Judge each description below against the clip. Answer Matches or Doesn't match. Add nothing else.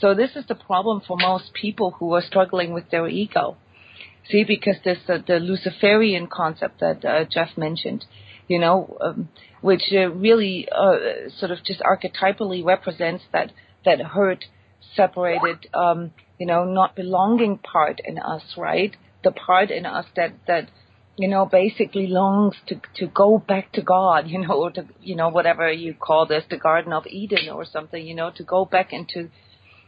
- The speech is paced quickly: Doesn't match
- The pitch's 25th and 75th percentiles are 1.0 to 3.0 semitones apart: Matches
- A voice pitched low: Doesn't match